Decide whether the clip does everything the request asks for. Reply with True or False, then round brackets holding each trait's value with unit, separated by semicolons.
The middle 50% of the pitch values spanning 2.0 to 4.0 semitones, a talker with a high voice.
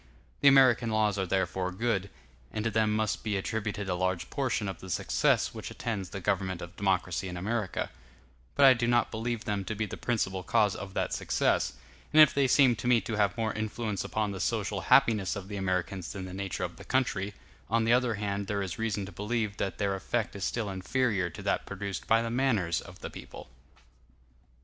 False (3.1 semitones; 105 Hz)